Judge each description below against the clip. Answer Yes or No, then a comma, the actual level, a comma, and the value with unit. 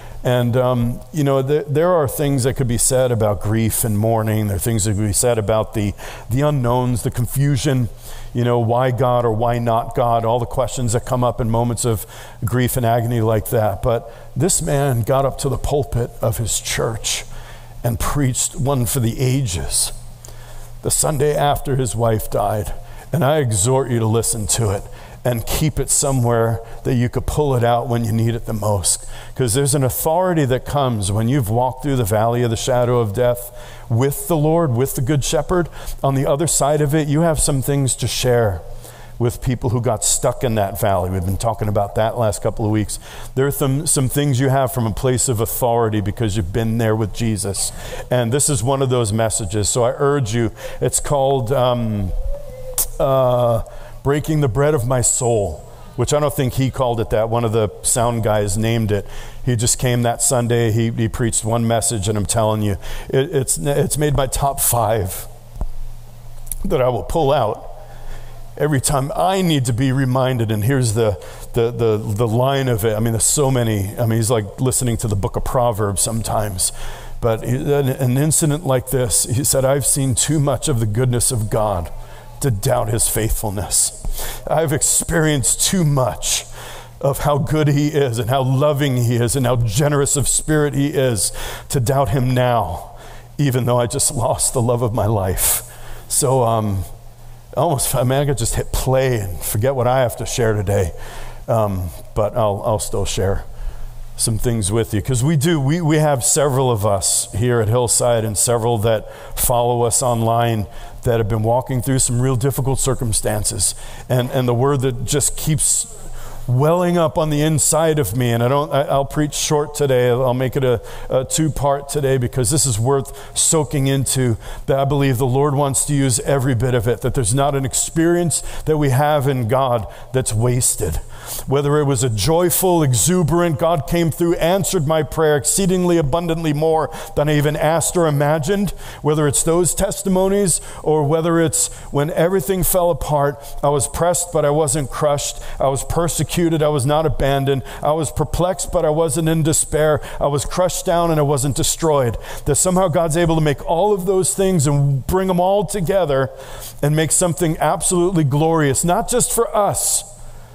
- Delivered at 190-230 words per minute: Yes, average, 195 wpm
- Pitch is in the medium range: No, low, 125 Hz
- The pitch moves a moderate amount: Yes, average, 3.8 semitones